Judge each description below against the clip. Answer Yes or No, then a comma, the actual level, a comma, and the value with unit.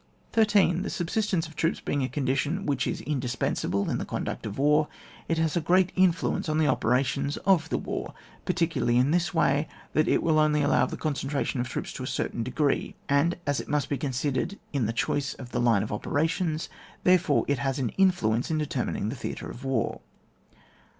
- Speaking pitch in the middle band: Yes, medium, 145 Hz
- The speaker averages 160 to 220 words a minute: Yes, fast, 205 wpm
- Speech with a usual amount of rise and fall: Yes, average, 4.0 semitones